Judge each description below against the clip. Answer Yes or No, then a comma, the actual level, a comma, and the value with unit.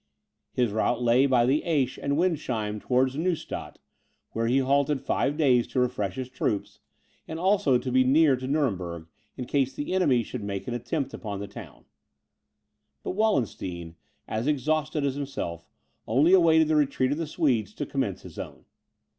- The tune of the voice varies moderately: Yes, average, 4.4 semitones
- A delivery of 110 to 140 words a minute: No, average, 170 wpm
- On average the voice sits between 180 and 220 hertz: No, low, 130 Hz